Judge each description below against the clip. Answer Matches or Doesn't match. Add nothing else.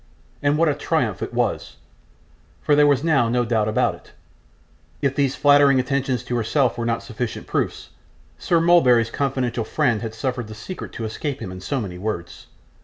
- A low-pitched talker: Matches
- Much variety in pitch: Doesn't match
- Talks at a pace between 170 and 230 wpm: Matches